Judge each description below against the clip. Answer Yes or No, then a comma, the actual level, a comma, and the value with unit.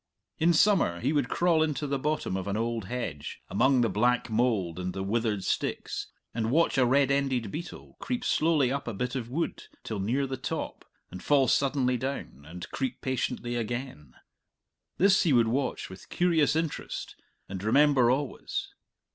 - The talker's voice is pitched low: Yes, low, 125 Hz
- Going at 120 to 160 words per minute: No, average, 170 wpm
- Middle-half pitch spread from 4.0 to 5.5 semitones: Yes, average, 4.7 semitones